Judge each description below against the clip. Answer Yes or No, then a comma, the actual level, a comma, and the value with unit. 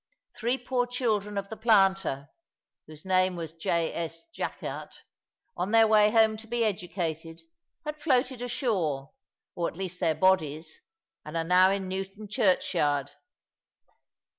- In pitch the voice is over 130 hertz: Yes, high, 190 Hz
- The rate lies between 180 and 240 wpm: No, average, 140 wpm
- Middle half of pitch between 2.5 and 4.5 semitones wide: No, average, 5.0 semitones